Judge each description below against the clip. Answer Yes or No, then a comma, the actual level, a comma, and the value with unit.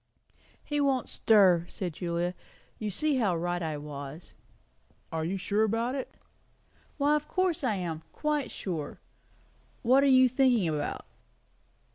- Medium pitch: No, high, 205 Hz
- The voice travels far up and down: Yes, wide, 7.8 semitones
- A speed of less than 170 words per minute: Yes, average, 140 wpm